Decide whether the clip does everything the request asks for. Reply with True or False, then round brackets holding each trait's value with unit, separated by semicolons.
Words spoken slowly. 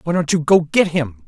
False (280 wpm)